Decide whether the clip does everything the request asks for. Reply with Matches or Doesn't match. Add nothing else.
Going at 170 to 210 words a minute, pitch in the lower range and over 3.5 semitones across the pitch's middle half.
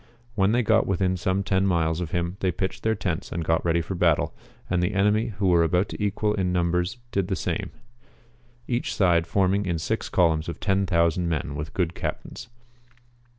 Doesn't match